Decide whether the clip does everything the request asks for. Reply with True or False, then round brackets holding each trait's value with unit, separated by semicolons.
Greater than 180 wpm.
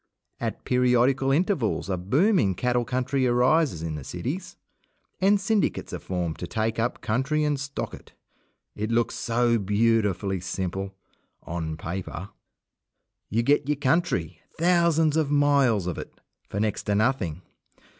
False (145 wpm)